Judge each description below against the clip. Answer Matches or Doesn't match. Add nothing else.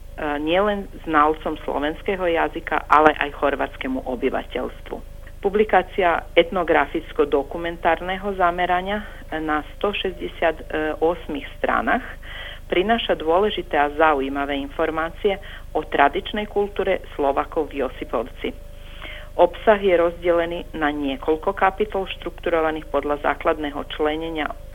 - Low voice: Doesn't match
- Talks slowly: Matches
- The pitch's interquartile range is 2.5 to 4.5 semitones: Matches